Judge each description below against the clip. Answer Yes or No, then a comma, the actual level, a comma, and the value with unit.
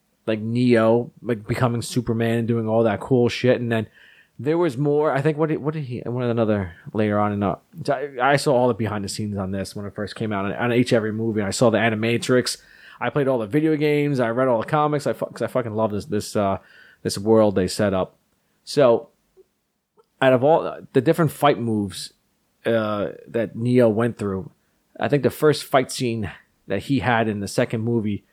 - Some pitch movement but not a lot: Yes, average, 3.5 semitones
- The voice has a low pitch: Yes, low, 115 Hz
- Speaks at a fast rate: Yes, fast, 215 wpm